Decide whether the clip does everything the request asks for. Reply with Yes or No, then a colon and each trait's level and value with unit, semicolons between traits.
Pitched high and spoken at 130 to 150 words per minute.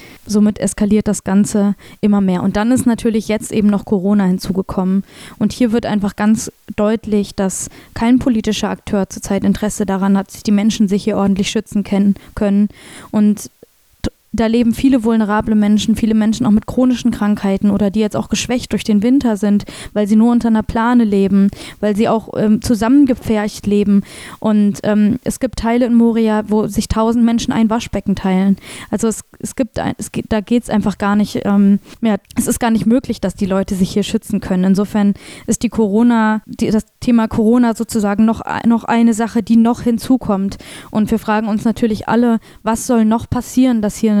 No: high, 215 Hz; fast, 190 wpm